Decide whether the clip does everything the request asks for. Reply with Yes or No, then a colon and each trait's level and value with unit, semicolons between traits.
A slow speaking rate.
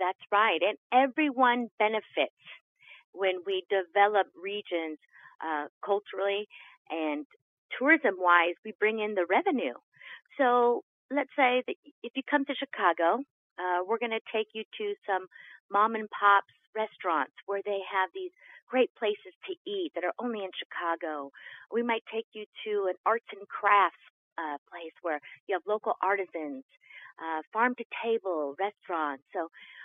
No: average, 150 wpm